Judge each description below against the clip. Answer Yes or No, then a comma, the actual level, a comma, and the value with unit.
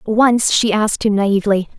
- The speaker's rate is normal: Yes, average, 170 wpm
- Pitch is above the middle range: Yes, high, 210 Hz